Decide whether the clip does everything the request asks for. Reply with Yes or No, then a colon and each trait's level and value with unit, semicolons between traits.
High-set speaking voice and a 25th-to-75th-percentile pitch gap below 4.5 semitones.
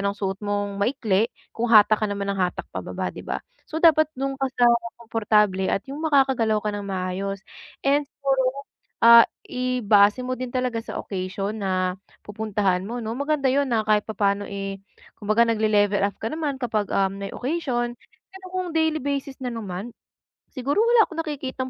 No: high, 225 Hz; average, 4.8 semitones